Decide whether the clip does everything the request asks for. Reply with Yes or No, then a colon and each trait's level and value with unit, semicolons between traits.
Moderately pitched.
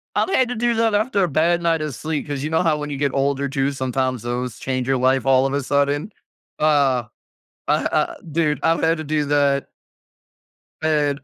Yes: medium, 145 Hz